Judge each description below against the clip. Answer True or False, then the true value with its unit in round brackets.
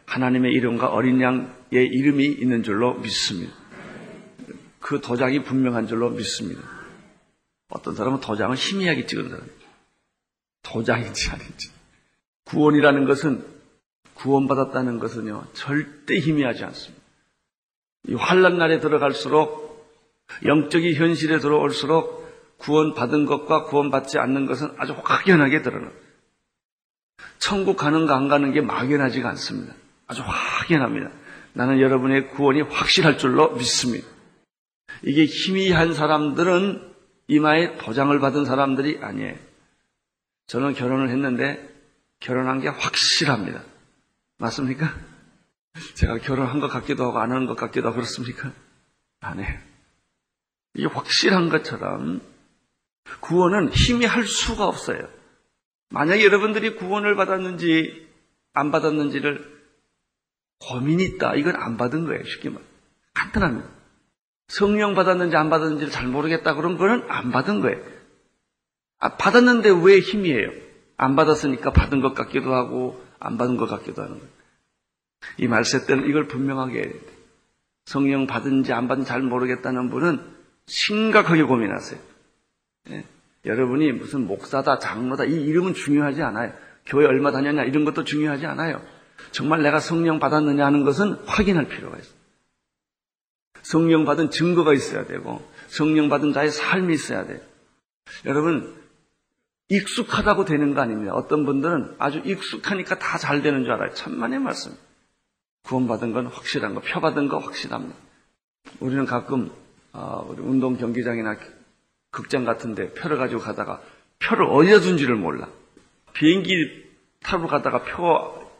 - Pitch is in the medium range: True (145 Hz)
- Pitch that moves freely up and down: False (3.9 semitones)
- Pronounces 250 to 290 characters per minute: False (305 characters per minute)